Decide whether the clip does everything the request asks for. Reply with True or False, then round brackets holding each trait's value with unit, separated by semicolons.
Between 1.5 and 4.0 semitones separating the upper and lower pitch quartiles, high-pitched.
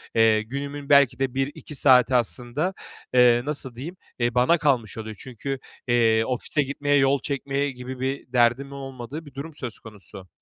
False (2.8 semitones; 130 Hz)